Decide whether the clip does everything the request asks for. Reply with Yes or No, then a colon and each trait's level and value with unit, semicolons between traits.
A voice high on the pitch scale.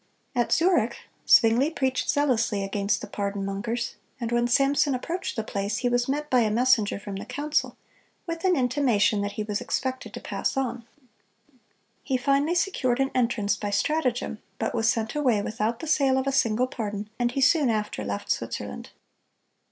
Yes: high, 240 Hz